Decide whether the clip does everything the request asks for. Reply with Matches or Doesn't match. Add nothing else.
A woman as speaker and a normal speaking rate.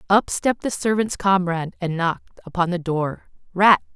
Matches